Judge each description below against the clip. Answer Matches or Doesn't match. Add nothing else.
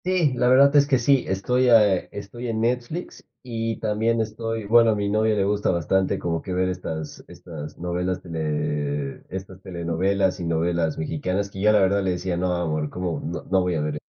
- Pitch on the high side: Doesn't match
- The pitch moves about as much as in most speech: Matches